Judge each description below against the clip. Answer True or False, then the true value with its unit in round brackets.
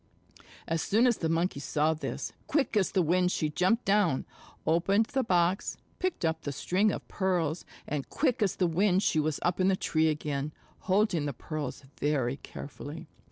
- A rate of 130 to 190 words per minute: True (180 wpm)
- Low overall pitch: False (170 Hz)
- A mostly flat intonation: False (4.2 semitones)